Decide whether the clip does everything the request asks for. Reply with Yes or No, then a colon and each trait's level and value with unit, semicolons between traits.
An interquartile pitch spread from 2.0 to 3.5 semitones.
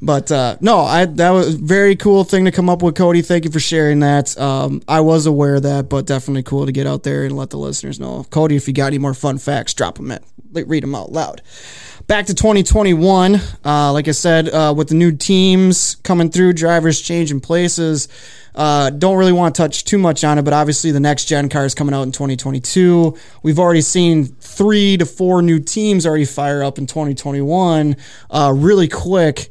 No: average, 3.9 semitones